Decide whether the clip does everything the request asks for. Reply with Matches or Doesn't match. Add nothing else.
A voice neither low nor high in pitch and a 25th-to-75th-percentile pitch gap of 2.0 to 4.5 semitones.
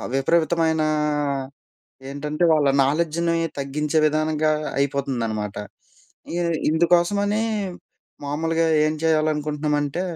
Matches